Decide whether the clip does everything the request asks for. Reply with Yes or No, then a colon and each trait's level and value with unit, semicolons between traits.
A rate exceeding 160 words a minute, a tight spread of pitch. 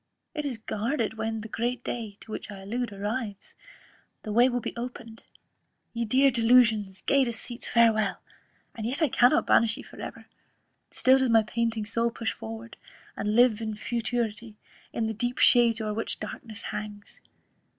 Yes: average, 170 wpm; narrow, 2.2 semitones